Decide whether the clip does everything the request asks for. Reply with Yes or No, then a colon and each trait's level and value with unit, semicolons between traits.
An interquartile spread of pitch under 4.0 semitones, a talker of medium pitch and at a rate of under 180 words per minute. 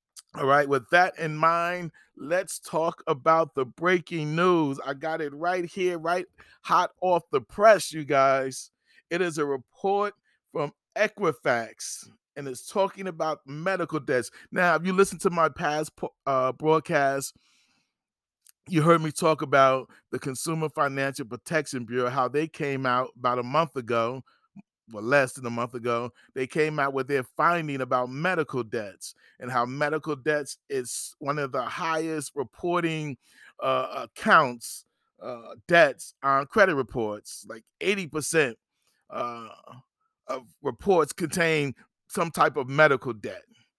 No: average, 4.4 semitones; medium, 155 Hz; average, 145 wpm